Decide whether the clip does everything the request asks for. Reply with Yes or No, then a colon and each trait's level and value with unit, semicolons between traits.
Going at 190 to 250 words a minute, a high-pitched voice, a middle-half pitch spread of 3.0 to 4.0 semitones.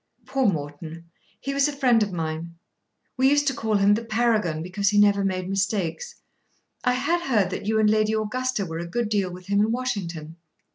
No: average, 200 wpm; high, 205 Hz; average, 5.1 semitones